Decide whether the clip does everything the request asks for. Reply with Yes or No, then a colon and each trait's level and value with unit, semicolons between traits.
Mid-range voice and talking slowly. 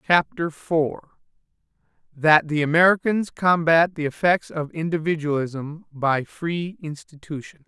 Yes: medium, 160 Hz; slow, 100 wpm